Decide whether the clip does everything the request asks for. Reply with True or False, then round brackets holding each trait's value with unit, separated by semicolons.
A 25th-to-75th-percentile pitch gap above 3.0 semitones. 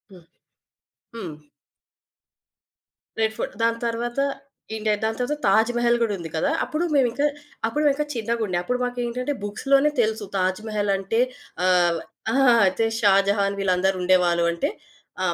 True (4.0 semitones)